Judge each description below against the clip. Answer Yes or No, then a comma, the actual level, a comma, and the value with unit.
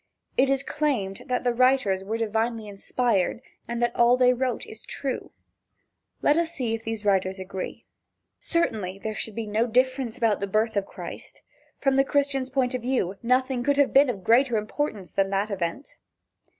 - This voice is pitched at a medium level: No, high, 235 Hz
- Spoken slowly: No, average, 180 wpm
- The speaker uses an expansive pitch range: No, average, 4.1 semitones